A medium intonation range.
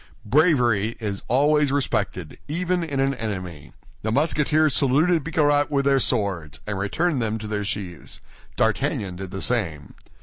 No: wide, 6.6 semitones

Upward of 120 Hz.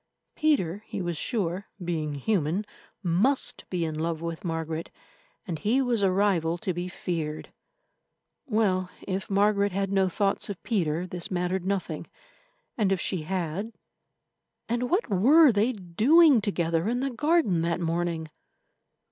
Yes: medium, 185 Hz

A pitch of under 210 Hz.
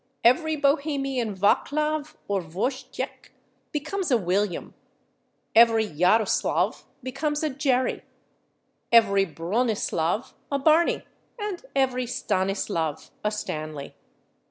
No: high, 235 Hz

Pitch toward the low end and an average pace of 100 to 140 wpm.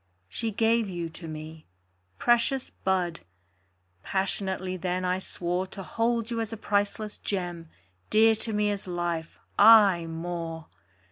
No: high, 190 Hz; slow, 135 wpm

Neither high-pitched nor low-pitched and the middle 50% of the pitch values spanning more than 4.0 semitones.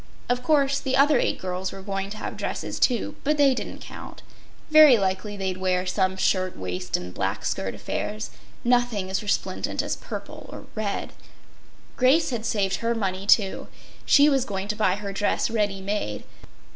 No: high, 205 Hz; average, 4.6 semitones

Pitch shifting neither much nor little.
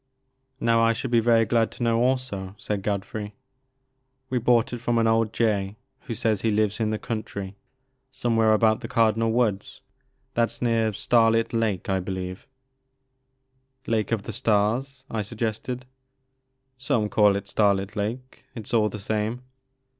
No: narrow, 2.3 semitones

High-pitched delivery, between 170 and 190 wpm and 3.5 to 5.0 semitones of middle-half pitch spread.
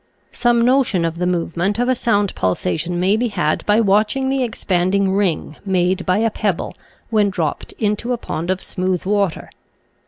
Yes: high, 200 Hz; average, 180 wpm; average, 3.8 semitones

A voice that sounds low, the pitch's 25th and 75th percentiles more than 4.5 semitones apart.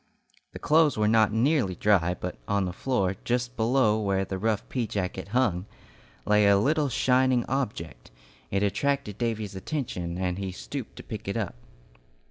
Yes: low, 105 Hz; average, 4.9 semitones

